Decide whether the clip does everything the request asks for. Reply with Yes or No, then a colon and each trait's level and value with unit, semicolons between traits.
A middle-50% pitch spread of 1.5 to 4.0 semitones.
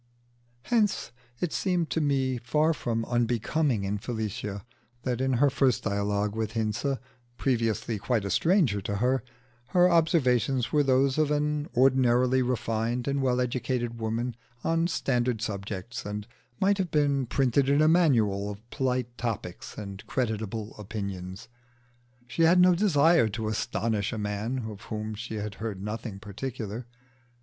No: average, 4.5 semitones